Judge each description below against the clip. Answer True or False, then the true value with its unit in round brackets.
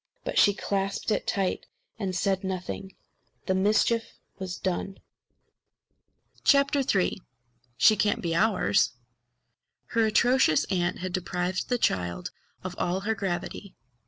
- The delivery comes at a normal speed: False (120 wpm)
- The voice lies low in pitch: False (190 Hz)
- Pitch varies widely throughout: False (2.8 semitones)